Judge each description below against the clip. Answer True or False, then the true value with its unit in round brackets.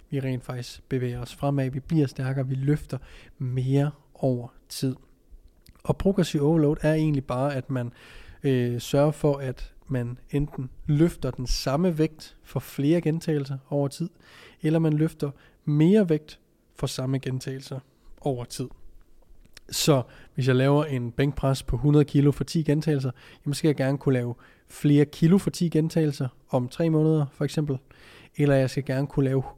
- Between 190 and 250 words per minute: False (165 wpm)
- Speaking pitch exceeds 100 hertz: True (140 Hz)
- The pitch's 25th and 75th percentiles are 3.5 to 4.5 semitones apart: False (2.6 semitones)